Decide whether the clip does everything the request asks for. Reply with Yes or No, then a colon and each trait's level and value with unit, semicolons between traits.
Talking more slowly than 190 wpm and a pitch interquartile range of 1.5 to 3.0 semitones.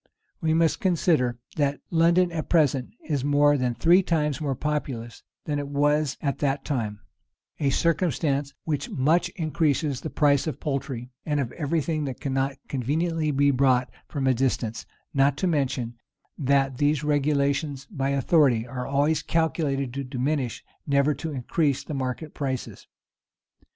Yes: average, 155 wpm; narrow, 2.6 semitones